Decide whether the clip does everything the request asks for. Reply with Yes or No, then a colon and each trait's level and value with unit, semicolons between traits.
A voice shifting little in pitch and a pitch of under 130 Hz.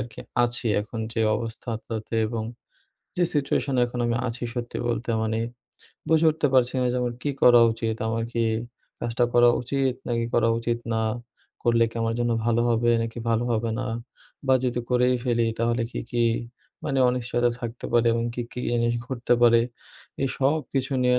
Yes: narrow, 1.3 semitones; low, 120 Hz